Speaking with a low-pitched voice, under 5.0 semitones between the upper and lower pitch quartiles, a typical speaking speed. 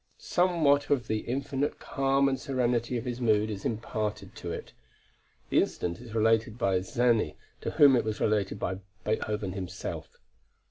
Yes: low, 115 Hz; average, 4.0 semitones; average, 155 wpm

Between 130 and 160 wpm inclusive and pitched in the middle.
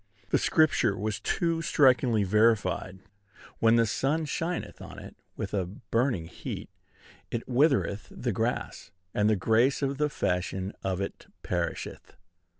No: average, 140 wpm; low, 115 Hz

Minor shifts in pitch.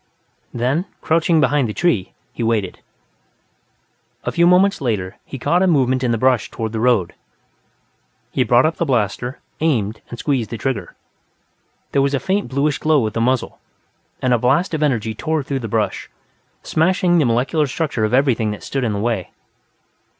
No: average, 5.1 semitones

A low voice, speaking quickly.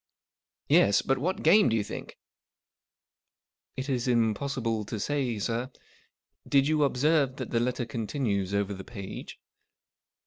No: low, 125 Hz; average, 150 wpm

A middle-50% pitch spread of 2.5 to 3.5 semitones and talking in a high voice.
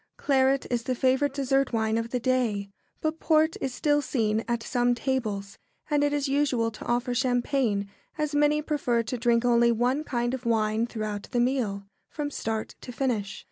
Yes: average, 3.2 semitones; high, 245 Hz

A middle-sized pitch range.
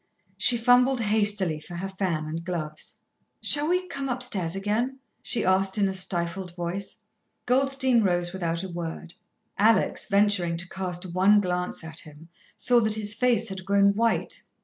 Yes: average, 4.6 semitones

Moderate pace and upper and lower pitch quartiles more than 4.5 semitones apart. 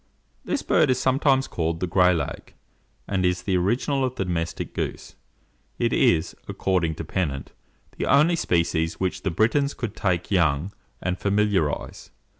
Yes: average, 155 wpm; average, 5.0 semitones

